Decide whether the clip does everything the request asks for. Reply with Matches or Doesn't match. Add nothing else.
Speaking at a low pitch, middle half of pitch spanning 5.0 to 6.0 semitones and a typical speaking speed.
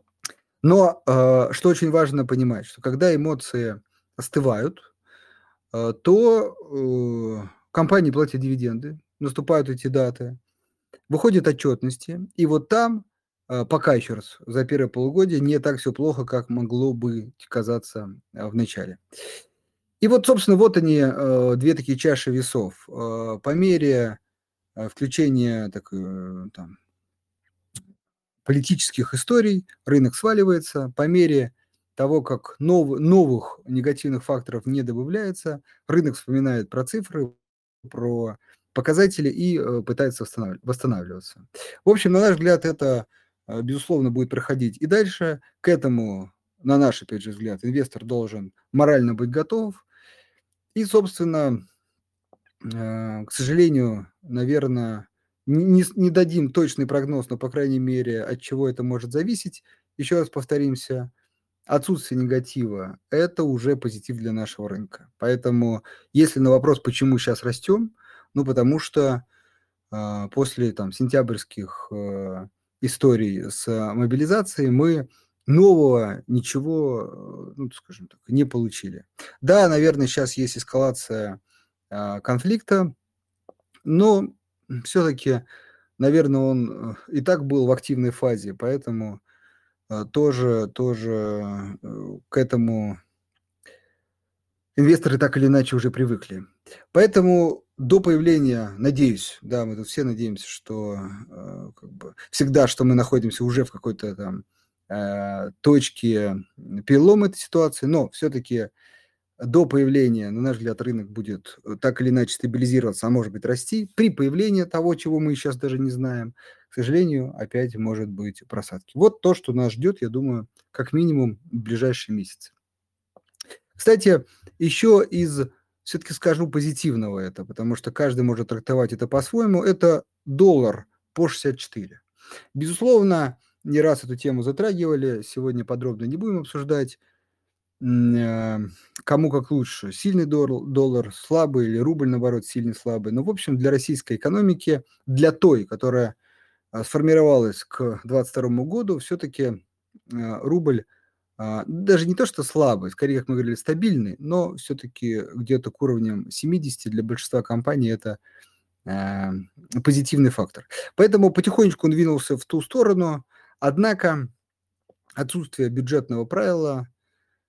Matches